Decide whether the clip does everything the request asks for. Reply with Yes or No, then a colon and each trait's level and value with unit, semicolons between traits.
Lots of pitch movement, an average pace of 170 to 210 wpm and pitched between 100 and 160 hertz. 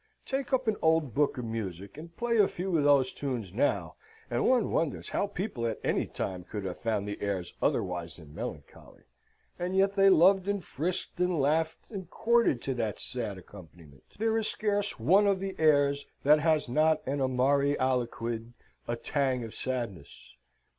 Yes: wide, 8.4 semitones; average, 180 wpm; medium, 140 Hz